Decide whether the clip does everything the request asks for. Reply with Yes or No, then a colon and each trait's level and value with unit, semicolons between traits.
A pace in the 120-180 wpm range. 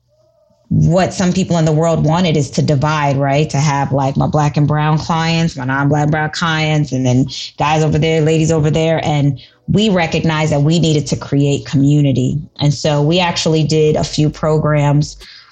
No: average, 190 wpm